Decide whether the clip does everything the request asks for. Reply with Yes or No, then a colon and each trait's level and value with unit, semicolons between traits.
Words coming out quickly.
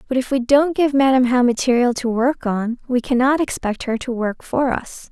Yes: fast, 225 wpm